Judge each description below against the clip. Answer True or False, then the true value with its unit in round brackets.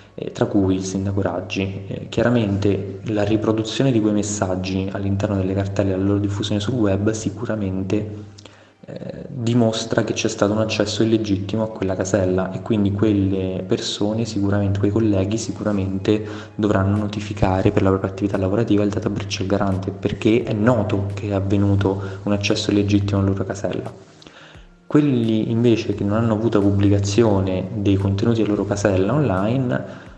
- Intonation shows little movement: True (2.1 semitones)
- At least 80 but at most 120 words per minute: False (155 wpm)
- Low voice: True (105 Hz)